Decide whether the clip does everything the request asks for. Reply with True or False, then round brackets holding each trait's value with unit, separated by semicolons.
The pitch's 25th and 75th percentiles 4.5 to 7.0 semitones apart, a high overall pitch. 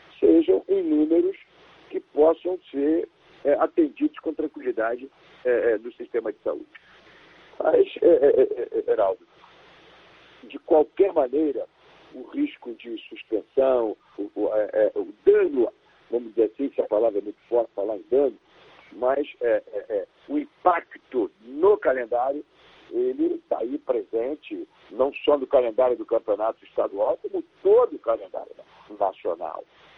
True (5.2 semitones; 395 Hz)